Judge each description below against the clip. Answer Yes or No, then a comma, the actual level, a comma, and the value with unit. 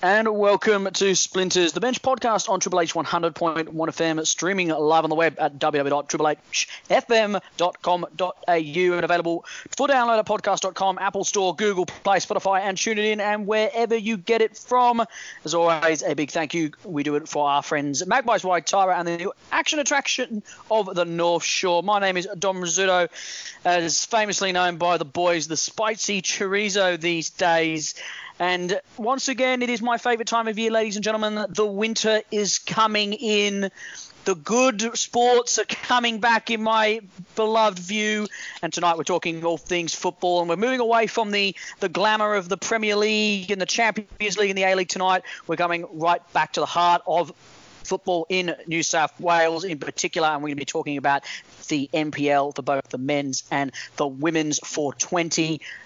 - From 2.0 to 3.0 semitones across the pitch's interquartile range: No, average, 4.5 semitones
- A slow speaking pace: No, average, 180 wpm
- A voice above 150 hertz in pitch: Yes, medium, 185 Hz